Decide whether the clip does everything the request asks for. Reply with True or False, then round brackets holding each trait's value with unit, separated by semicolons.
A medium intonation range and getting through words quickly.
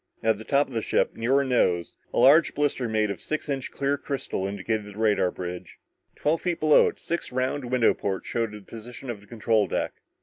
True (5.0 semitones; 215 wpm)